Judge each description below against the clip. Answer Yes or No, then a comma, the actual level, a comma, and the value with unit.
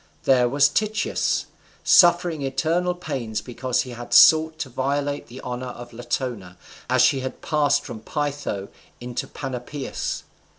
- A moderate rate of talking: No, slow, 130 wpm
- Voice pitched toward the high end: No, low, 135 Hz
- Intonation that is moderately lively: Yes, average, 3.2 semitones